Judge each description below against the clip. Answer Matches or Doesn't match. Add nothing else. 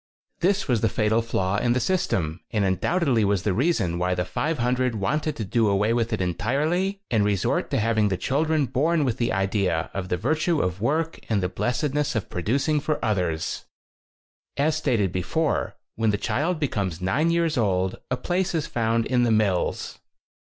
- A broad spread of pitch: Matches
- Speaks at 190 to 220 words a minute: Matches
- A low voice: Matches